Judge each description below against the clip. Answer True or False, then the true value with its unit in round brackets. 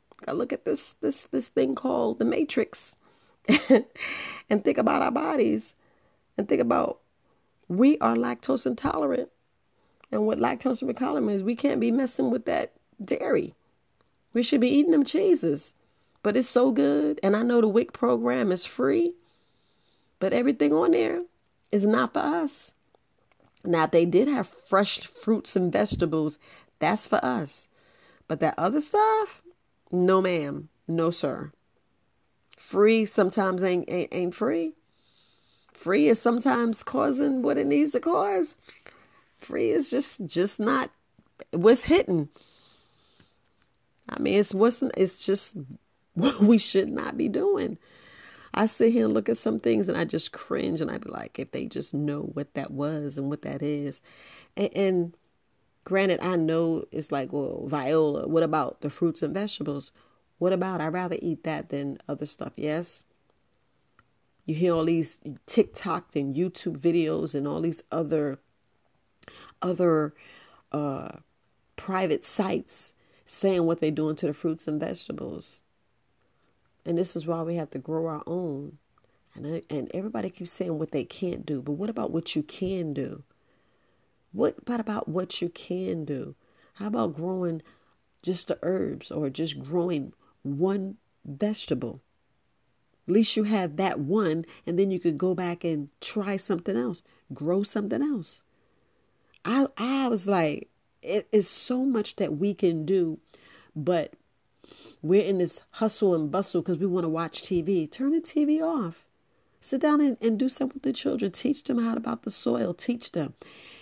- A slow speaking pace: False (160 wpm)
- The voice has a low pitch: False (180 Hz)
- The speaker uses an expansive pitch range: True (6.4 semitones)